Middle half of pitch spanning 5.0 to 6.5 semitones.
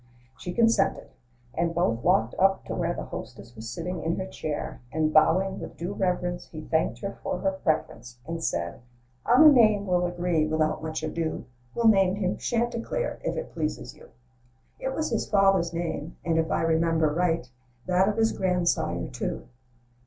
No: average, 3.5 semitones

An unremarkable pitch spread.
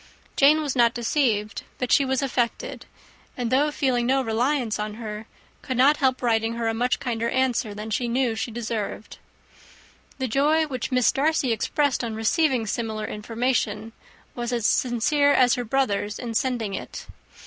Yes: average, 3.0 semitones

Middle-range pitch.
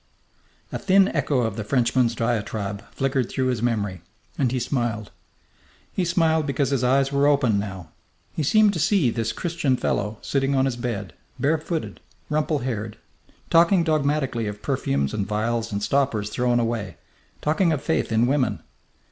No: low, 125 Hz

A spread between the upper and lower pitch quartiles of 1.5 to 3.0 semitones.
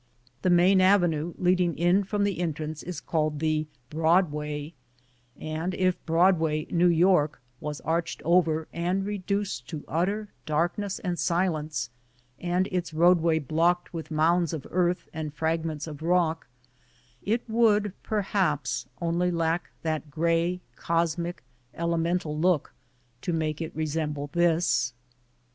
Yes: narrow, 2.4 semitones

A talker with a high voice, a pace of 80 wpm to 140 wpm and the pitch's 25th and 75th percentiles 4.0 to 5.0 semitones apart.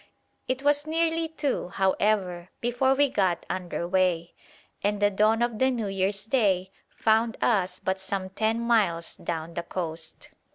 No: high, 205 Hz; average, 155 wpm; average, 4.6 semitones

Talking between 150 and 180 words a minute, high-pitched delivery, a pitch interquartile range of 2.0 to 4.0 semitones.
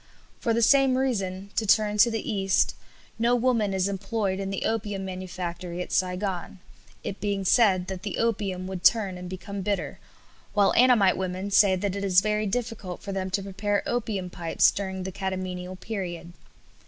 Yes: average, 175 wpm; high, 195 Hz; narrow, 2.4 semitones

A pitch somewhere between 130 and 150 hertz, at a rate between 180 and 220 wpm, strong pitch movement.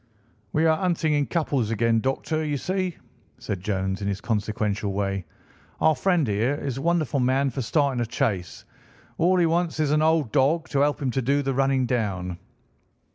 Yes: low, 135 Hz; average, 185 wpm; wide, 6.3 semitones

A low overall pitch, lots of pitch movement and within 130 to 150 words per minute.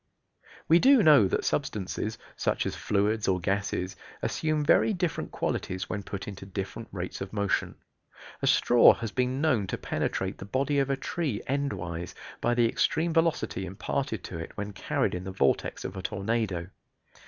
No: low, 105 Hz; wide, 6.5 semitones; average, 170 wpm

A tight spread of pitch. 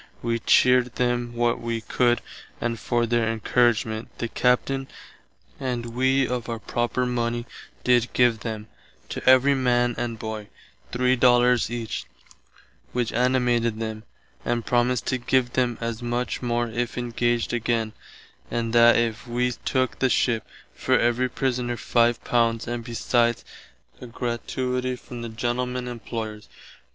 Yes: narrow, 1.2 semitones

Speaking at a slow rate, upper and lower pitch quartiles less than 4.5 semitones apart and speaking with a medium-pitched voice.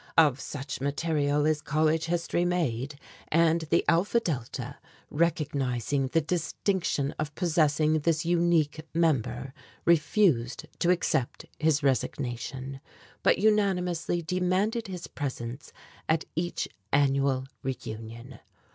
Yes: slow, 105 wpm; average, 3.9 semitones; medium, 155 Hz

